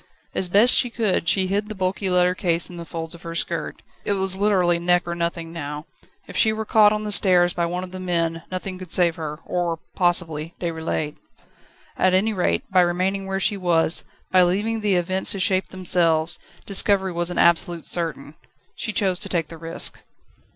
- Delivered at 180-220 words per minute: Yes, average, 195 wpm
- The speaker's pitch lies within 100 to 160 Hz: No, medium, 180 Hz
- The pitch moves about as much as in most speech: No, narrow, 2.3 semitones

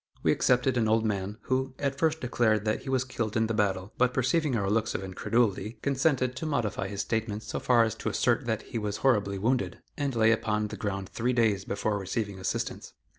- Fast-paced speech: Yes, fast, 215 wpm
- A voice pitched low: Yes, low, 110 Hz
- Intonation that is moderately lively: Yes, average, 3.7 semitones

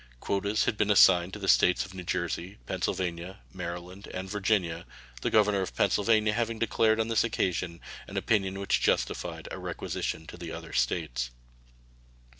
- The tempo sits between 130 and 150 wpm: No, average, 160 wpm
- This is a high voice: No, very low, 95 Hz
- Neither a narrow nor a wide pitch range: Yes, average, 3.2 semitones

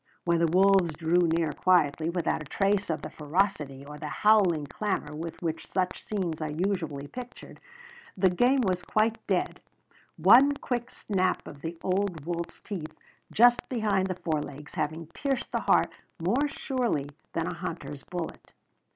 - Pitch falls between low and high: Yes, medium, 175 Hz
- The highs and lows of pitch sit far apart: No, average, 4.3 semitones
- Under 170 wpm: Yes, average, 160 wpm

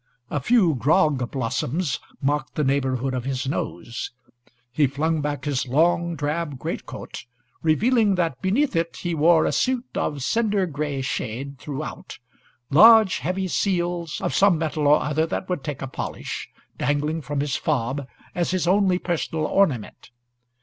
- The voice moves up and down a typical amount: Yes, average, 4.4 semitones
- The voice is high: No, medium, 155 Hz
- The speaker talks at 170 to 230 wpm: No, average, 150 wpm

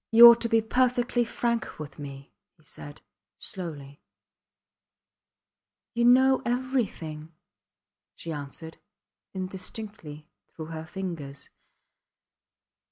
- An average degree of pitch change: No, wide, 7.6 semitones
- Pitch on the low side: No, medium, 185 Hz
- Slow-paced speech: Yes, slow, 95 wpm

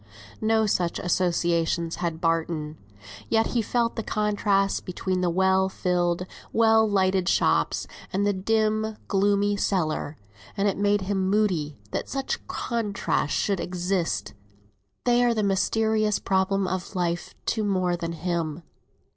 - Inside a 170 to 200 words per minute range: No, slow, 135 wpm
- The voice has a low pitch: No, high, 190 Hz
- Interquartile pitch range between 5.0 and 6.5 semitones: No, average, 3.3 semitones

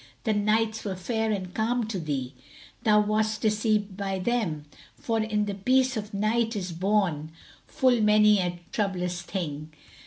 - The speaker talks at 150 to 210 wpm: Yes, average, 155 wpm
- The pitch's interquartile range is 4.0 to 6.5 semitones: No, average, 3.0 semitones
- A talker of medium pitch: No, high, 210 Hz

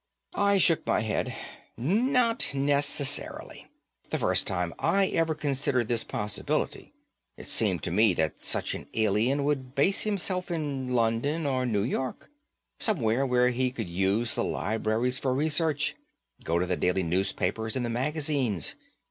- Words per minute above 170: No, average, 145 wpm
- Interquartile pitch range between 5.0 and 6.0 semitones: Yes, average, 5.3 semitones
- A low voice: Yes, low, 130 Hz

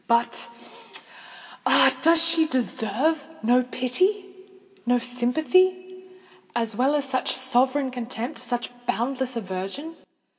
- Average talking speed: No, slow, 85 wpm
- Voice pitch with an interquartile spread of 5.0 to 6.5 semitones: Yes, wide, 5.4 semitones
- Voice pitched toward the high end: Yes, very high, 260 Hz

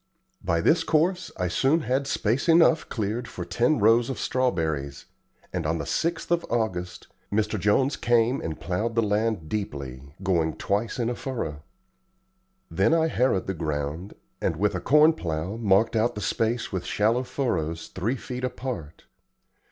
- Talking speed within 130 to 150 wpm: No, average, 160 wpm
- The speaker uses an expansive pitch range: Yes, wide, 6.5 semitones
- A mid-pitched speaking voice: No, low, 110 Hz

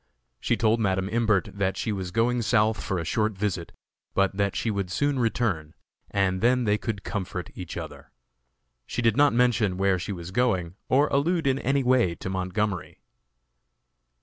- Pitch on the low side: Yes, low, 105 Hz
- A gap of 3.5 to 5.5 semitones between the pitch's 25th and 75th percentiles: Yes, average, 4.2 semitones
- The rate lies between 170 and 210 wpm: Yes, average, 175 wpm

